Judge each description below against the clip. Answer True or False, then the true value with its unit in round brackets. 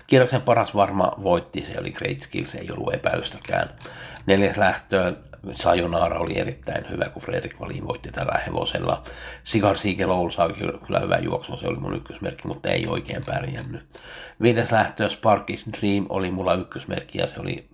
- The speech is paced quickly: True (160 wpm)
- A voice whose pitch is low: True (100 Hz)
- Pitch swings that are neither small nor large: True (3.0 semitones)